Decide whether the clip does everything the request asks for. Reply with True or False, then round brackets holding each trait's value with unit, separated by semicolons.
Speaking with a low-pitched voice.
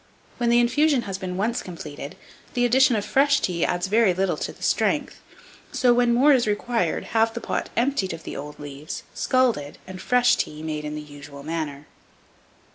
False (195 Hz)